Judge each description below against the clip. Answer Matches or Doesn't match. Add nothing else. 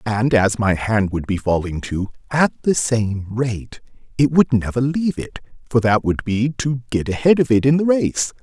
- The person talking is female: Doesn't match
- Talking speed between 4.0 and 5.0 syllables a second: Matches